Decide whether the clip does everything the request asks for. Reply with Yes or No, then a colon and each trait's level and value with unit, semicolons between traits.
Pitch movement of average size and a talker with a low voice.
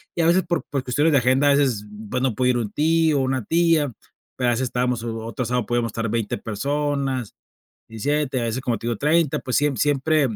Yes: average, 3.6 semitones; low, 130 Hz